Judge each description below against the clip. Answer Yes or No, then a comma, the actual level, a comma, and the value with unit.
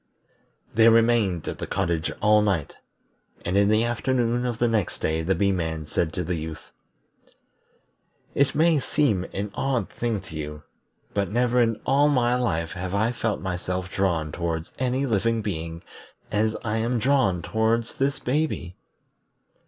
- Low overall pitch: Yes, low, 105 Hz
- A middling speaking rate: Yes, average, 160 wpm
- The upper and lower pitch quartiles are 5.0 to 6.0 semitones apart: Yes, average, 5.3 semitones